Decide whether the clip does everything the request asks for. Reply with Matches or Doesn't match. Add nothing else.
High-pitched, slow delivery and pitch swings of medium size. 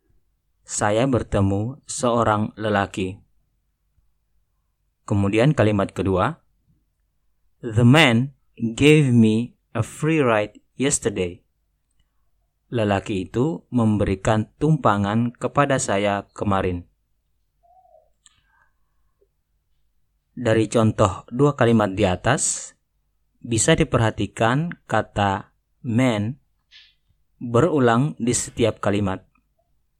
Doesn't match